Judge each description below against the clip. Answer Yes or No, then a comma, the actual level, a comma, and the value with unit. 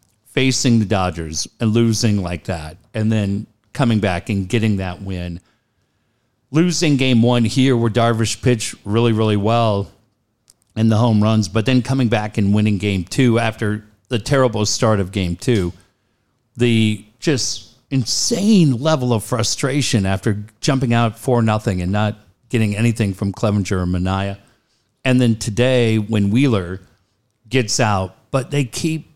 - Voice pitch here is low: Yes, low, 110 Hz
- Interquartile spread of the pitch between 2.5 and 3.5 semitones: Yes, average, 3.0 semitones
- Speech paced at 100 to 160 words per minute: Yes, average, 150 wpm